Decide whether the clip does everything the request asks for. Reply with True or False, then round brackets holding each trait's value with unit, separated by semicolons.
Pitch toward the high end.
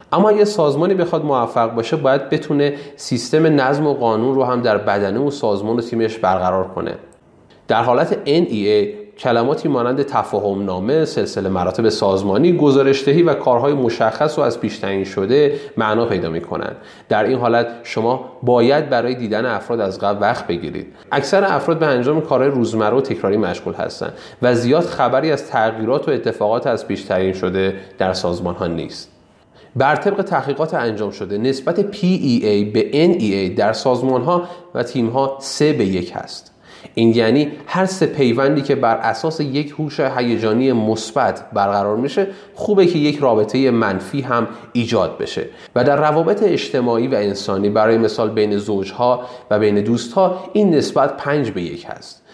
False (125 Hz)